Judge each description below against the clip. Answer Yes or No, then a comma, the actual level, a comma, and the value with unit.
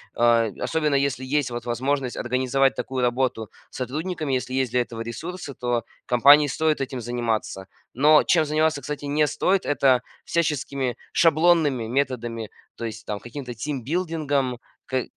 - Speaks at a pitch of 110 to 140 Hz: Yes, low, 135 Hz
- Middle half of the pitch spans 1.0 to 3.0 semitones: No, average, 3.7 semitones